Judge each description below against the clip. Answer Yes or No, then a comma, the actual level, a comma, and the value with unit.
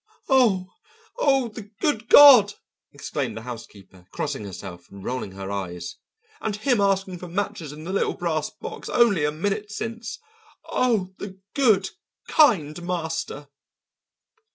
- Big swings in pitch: Yes, wide, 7.5 semitones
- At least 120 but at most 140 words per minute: Yes, slow, 135 wpm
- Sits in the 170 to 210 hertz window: Yes, medium, 185 Hz